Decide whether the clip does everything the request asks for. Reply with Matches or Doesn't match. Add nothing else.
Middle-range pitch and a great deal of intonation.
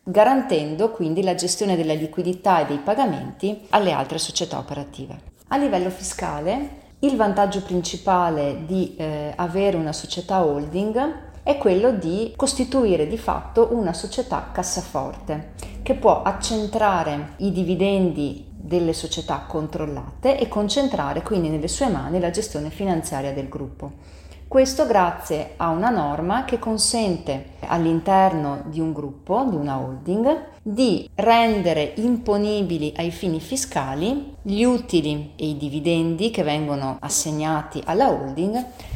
Matches